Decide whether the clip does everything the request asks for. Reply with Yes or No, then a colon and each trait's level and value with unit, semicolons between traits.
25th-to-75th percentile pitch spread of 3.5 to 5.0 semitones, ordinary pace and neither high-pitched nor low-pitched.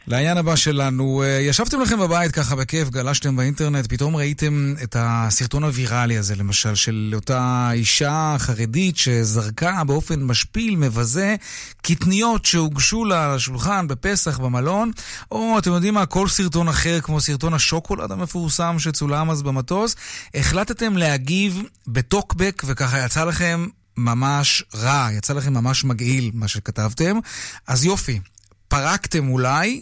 No: wide, 5.6 semitones; average, 130 wpm; medium, 145 Hz